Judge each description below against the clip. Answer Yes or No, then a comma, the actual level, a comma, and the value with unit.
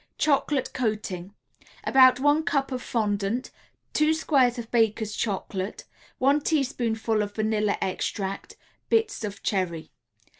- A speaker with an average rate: No, slow, 115 wpm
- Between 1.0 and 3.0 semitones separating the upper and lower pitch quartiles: No, average, 4.8 semitones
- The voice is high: Yes, high, 225 Hz